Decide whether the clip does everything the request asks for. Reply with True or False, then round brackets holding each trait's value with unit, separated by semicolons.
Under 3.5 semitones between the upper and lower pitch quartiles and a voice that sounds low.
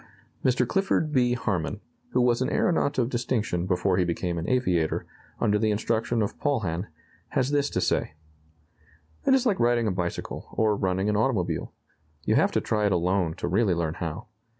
False (5.6 semitones; 105 Hz)